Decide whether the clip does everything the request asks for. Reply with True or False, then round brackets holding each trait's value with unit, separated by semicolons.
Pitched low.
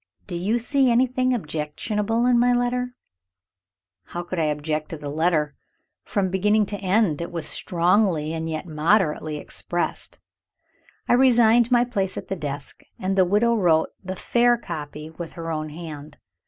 False (185 Hz)